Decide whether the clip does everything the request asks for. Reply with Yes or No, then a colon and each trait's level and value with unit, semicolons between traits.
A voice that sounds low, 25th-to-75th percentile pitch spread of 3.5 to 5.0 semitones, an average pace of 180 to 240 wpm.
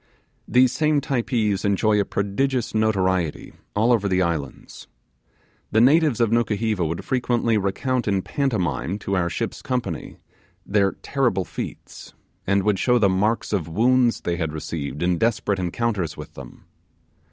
No: low, 105 Hz; average, 4.4 semitones; average, 145 wpm